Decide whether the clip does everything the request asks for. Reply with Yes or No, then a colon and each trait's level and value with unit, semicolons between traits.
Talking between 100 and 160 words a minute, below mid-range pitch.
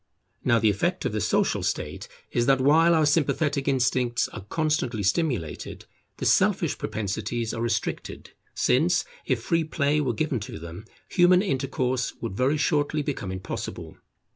Yes: average, 150 wpm; low, 130 Hz